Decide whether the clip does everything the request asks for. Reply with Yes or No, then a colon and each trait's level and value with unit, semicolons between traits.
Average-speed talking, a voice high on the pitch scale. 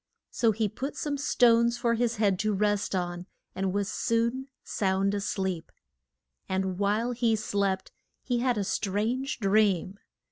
Yes: average, 150 wpm; high, 210 Hz